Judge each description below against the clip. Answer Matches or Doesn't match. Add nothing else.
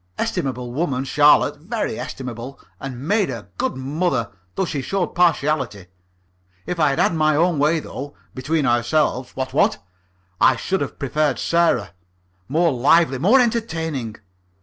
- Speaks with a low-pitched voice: Doesn't match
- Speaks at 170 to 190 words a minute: Doesn't match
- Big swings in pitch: Doesn't match